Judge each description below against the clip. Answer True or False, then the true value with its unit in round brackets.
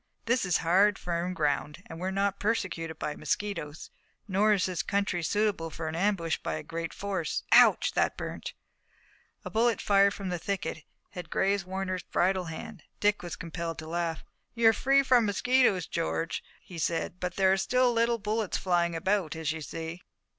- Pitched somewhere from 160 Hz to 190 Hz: True (185 Hz)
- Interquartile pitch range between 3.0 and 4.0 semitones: True (3.7 semitones)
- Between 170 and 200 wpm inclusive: True (175 wpm)